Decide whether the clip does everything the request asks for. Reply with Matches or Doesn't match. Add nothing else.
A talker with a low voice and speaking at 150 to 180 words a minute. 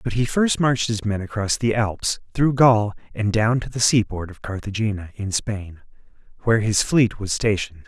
Doesn't match